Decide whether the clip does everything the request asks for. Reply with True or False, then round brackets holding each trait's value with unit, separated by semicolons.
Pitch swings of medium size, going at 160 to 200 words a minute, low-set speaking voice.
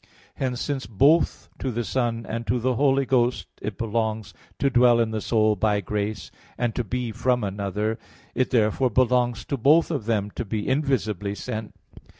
True (3.1 semitones; 175 wpm; 115 Hz)